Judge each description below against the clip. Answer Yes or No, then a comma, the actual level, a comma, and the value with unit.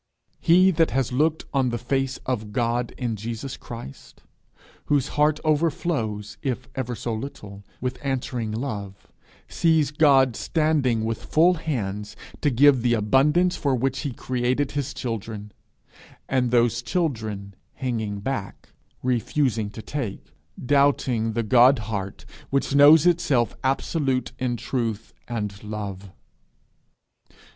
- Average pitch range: Yes, average, 4.3 semitones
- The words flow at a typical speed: No, slow, 125 wpm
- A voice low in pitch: Yes, low, 125 Hz